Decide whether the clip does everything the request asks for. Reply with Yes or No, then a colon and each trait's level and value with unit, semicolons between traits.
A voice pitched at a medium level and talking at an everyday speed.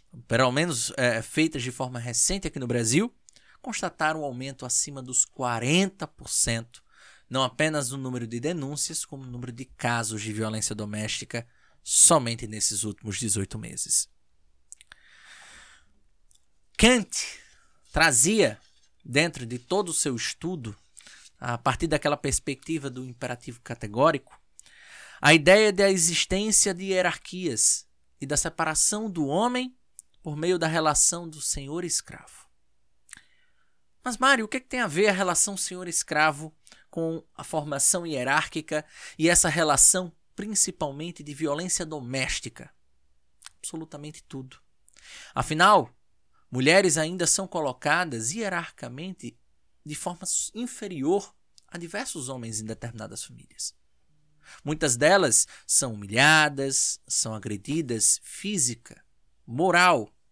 No: medium, 150 Hz; slow, 115 wpm